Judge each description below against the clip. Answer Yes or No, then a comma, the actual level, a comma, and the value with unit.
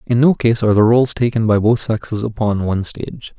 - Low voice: Yes, low, 110 Hz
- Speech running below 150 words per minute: No, fast, 230 wpm